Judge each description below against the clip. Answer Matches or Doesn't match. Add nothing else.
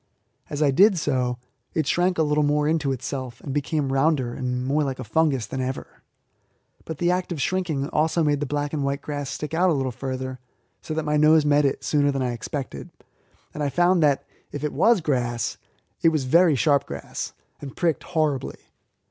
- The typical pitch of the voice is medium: Matches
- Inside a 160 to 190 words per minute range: Doesn't match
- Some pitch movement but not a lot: Matches